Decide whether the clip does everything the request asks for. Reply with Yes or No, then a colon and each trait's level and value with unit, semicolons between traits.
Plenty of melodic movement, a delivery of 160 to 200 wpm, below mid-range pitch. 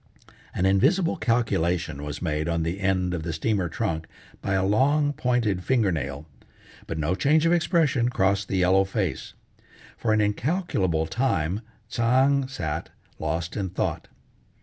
No: wide, 6.9 semitones; average, 145 wpm; very low, 95 Hz